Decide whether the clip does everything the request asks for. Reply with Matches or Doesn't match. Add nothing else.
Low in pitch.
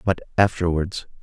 Matches